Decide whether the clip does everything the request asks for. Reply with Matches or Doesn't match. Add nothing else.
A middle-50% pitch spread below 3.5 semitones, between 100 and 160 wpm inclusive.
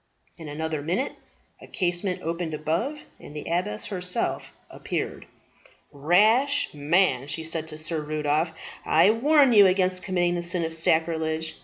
Matches